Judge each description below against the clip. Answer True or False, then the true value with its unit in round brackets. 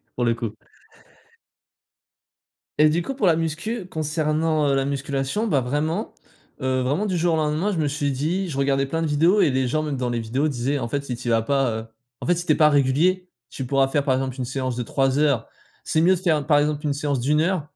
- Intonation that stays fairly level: False (3.4 semitones)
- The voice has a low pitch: False (145 Hz)